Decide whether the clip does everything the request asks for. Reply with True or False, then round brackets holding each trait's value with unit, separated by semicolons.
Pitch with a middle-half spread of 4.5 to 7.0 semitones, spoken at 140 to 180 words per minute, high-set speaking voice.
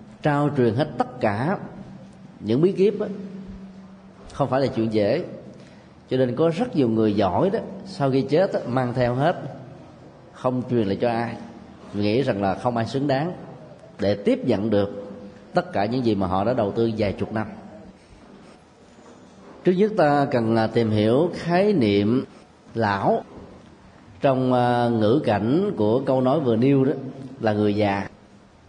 False (5.2 semitones; 165 wpm; 125 Hz)